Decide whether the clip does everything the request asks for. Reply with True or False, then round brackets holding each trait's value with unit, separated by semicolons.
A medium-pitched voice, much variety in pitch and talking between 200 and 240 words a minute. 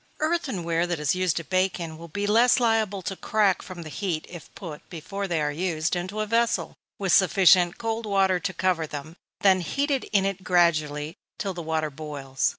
False (180 Hz; 3.7 semitones; 205 wpm)